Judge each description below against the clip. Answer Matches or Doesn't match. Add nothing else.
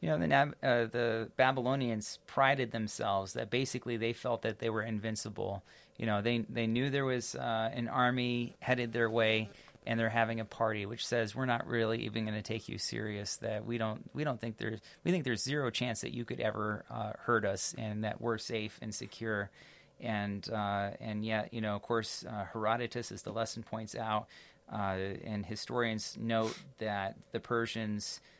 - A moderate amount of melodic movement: Doesn't match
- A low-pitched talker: Matches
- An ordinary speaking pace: Matches